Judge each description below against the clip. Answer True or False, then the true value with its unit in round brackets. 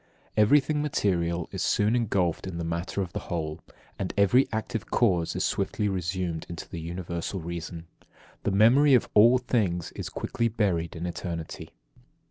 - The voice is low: True (95 Hz)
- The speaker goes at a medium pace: True (160 wpm)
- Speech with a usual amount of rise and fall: True (4.5 semitones)